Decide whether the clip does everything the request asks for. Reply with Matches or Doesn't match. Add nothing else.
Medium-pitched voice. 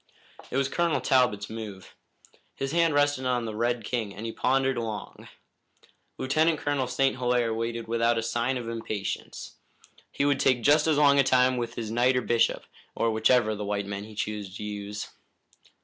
Doesn't match